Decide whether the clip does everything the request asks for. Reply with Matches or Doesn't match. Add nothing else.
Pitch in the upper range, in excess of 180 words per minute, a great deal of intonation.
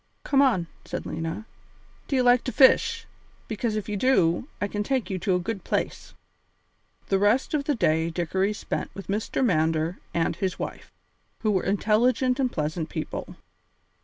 Doesn't match